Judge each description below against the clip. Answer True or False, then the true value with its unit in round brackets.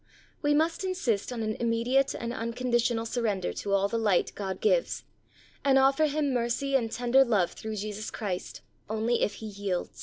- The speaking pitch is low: False (235 Hz)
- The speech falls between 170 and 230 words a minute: True (180 wpm)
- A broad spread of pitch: False (4.1 semitones)